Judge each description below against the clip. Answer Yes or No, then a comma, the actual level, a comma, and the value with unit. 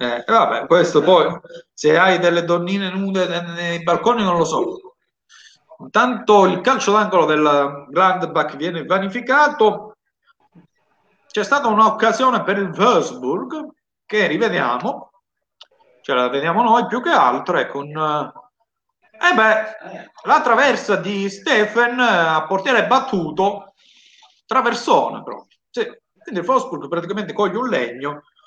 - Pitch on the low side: No, high, 210 Hz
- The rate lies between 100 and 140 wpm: Yes, average, 120 wpm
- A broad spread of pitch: Yes, wide, 6.8 semitones